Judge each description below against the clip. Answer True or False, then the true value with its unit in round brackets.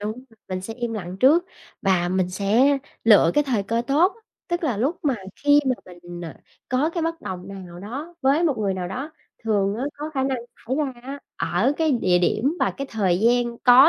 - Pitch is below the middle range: False (235 Hz)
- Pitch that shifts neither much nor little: False (6.6 semitones)